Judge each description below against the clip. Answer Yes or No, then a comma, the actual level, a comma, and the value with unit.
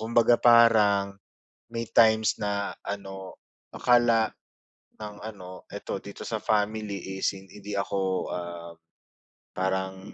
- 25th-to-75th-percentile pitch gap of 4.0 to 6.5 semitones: No, narrow, 2.4 semitones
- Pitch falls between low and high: No, low, 100 Hz